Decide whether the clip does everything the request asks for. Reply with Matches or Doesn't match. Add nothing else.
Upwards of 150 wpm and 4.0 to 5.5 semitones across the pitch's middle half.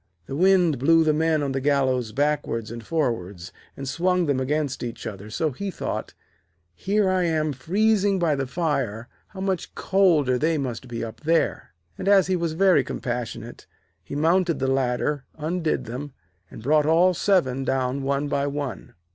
Matches